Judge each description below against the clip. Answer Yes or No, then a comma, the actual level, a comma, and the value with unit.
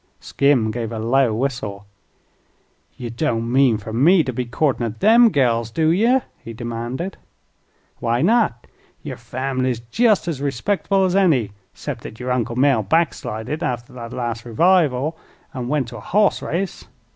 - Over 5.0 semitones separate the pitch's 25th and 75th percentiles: Yes, wide, 5.6 semitones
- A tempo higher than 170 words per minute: No, average, 155 wpm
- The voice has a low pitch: Yes, low, 125 Hz